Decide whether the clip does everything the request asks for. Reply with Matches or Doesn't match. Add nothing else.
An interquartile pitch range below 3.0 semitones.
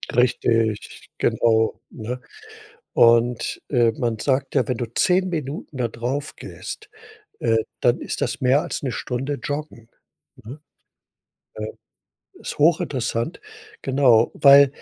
Doesn't match